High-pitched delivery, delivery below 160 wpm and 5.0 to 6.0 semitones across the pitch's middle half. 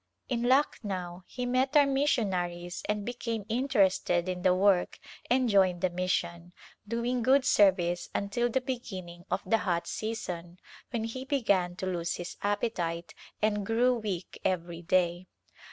Yes: high, 200 Hz; average, 150 wpm; average, 5.3 semitones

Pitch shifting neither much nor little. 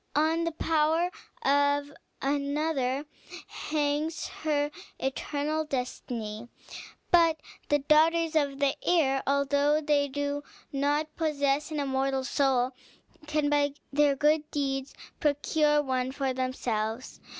No: narrow, 2.0 semitones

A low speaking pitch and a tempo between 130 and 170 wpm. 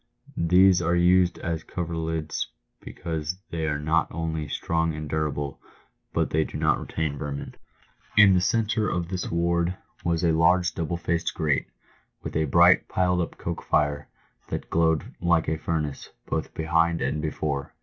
Yes: very low, 80 Hz; average, 160 wpm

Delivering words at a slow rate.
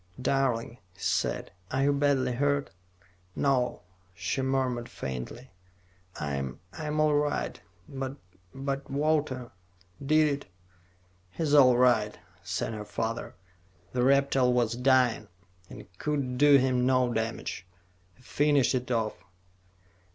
Yes: slow, 120 wpm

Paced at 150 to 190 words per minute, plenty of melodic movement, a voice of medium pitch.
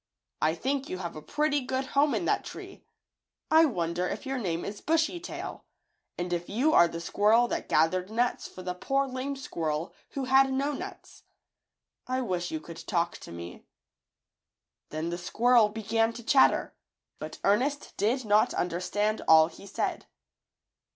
No: average, 165 wpm; wide, 7.4 semitones; high, 215 Hz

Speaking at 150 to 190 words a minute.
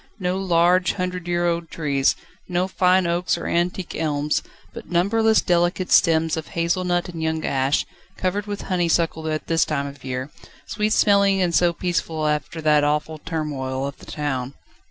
Yes: average, 170 wpm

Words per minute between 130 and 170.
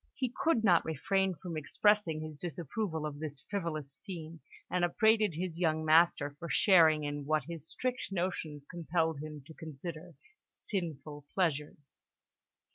Yes: average, 140 wpm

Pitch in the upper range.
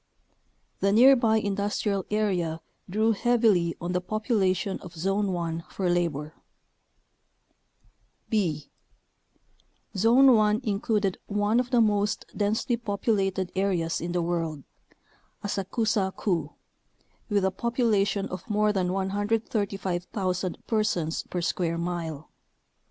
Yes: high, 195 Hz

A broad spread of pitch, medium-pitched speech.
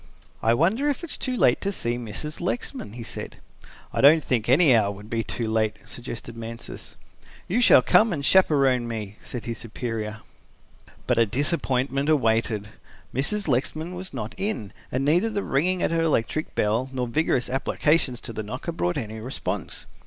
No: wide, 6.3 semitones; low, 130 Hz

